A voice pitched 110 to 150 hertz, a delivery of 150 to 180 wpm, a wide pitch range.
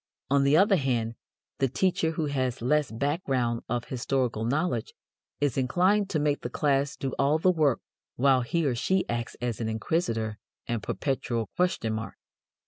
No: low, 135 Hz; average, 160 wpm; average, 4.7 semitones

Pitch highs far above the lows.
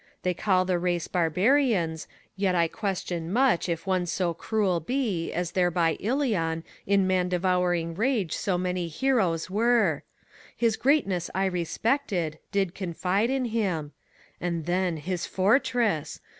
No: average, 3.9 semitones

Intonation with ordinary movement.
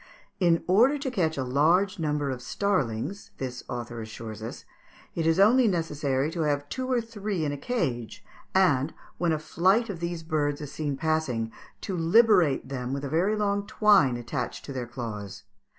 No: wide, 6.8 semitones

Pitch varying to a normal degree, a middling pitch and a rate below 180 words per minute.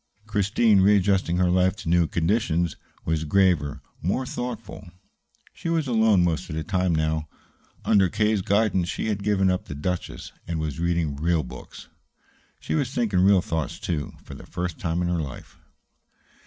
No: average, 3.9 semitones; very low, 90 Hz; average, 170 wpm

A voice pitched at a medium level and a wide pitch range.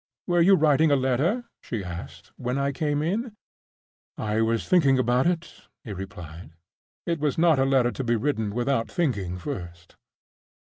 No: low, 130 Hz; wide, 6.7 semitones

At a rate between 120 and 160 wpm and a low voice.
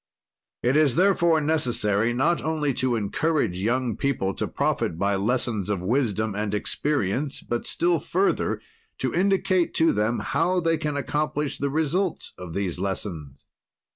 Yes: average, 145 wpm; low, 130 Hz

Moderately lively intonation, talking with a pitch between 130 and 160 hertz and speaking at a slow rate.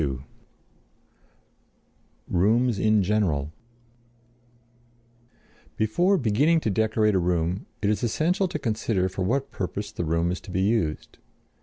No: average, 4.4 semitones; low, 105 Hz; slow, 125 wpm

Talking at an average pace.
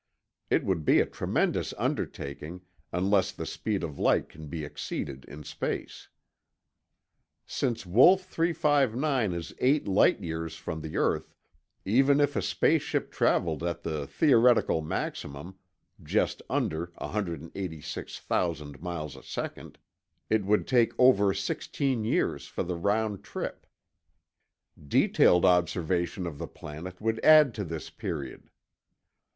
No: slow, 125 wpm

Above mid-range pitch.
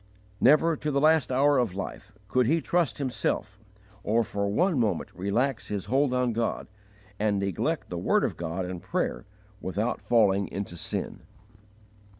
No: low, 115 Hz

